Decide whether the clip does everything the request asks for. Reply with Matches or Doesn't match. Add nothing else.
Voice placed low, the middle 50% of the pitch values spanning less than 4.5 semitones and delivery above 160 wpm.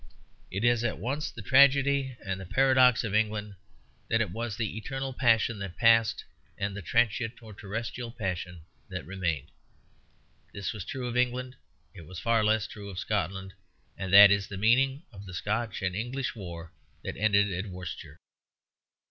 Matches